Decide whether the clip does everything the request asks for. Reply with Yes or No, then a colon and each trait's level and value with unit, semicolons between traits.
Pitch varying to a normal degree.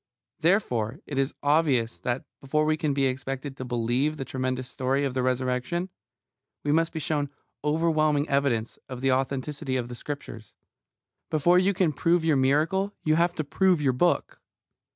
Yes: average, 3.4 semitones